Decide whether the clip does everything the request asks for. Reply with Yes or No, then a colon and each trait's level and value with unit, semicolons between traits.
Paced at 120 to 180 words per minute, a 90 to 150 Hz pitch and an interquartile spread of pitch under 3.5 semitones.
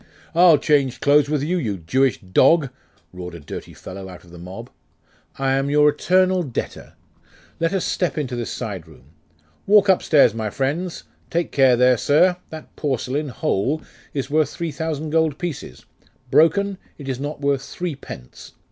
No: average, 165 wpm; medium, 140 Hz; average, 5.0 semitones